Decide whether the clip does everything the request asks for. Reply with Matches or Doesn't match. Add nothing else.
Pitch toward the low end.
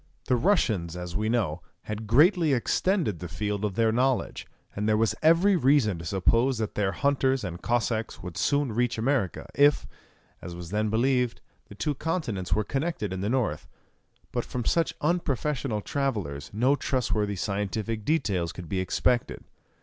Matches